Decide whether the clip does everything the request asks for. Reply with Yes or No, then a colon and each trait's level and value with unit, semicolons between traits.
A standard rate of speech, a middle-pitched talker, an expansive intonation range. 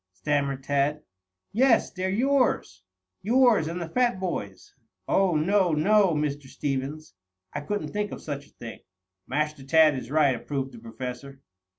Yes: average, 150 wpm; medium, 150 Hz; wide, 5.8 semitones